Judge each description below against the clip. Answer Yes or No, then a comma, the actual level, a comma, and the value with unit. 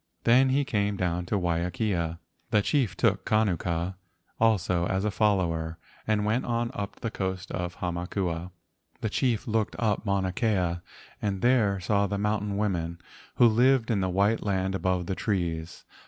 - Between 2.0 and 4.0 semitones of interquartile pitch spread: Yes, average, 3.6 semitones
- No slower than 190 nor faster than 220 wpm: No, average, 160 wpm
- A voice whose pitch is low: Yes, low, 100 Hz